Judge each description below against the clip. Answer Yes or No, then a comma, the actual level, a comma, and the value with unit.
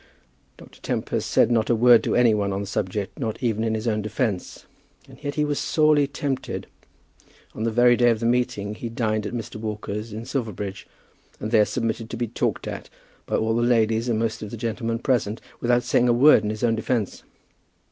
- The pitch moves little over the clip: Yes, narrow, 2.2 semitones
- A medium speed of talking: No, fast, 210 wpm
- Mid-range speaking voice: No, low, 115 Hz